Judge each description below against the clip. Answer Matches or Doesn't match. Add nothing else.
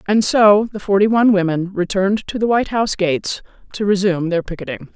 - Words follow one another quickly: Doesn't match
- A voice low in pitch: Doesn't match